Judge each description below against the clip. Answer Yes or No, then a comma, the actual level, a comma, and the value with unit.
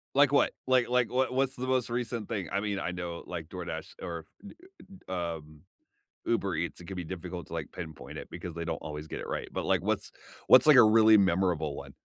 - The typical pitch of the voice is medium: No, very low, 95 Hz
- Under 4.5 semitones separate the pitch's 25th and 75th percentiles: No, wide, 6.3 semitones